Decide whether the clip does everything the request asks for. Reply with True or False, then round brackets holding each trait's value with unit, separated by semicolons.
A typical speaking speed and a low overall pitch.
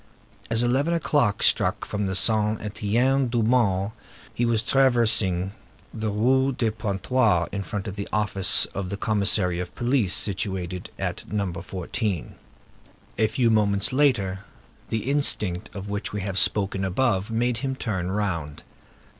True (145 wpm; 105 Hz)